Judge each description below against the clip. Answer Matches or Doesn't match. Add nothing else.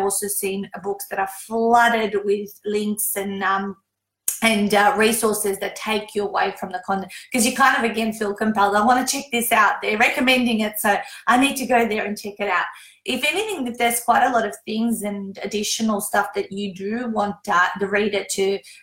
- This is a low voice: Doesn't match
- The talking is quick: Matches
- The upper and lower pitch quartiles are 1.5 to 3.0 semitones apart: Matches